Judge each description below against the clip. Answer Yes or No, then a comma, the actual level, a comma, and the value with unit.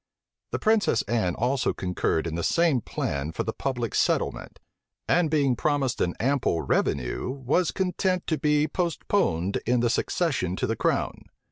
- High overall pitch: No, low, 130 Hz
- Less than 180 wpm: Yes, average, 155 wpm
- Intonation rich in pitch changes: Yes, wide, 8.5 semitones